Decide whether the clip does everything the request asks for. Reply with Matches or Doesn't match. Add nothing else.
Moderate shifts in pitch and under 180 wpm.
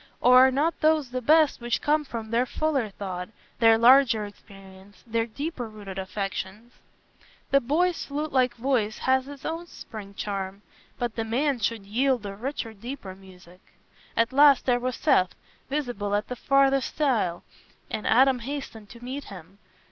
Matches